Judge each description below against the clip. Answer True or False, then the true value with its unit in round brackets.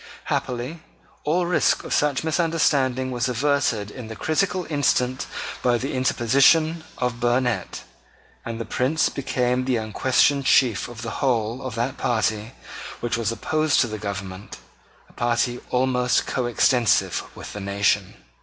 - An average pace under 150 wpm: True (140 wpm)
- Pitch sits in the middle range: False (125 Hz)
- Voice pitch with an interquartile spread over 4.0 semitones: False (3.2 semitones)